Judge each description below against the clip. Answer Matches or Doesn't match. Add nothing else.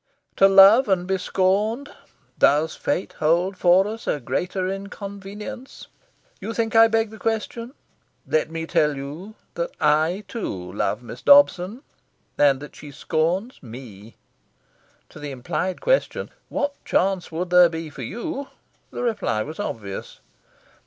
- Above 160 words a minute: Doesn't match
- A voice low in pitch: Doesn't match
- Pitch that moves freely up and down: Matches